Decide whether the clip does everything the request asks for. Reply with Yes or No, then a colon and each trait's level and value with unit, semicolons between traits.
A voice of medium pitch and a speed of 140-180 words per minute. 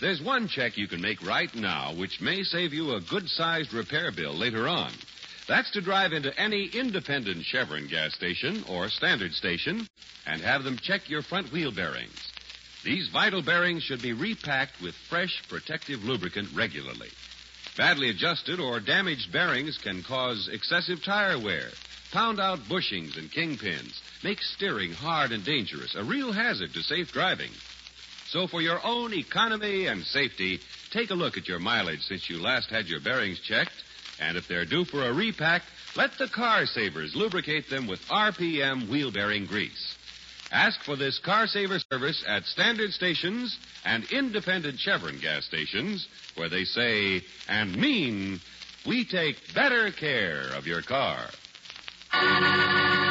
Yes: medium, 160 Hz; average, 160 wpm